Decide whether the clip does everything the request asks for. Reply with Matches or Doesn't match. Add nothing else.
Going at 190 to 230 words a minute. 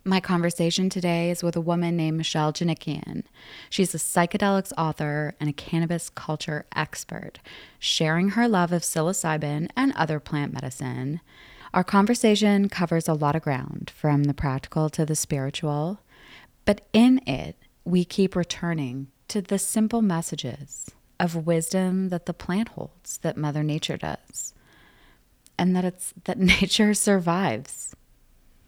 Doesn't match